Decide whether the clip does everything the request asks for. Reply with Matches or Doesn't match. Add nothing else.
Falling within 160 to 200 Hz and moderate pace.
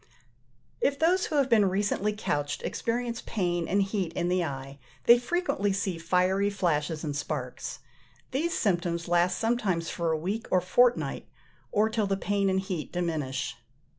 Matches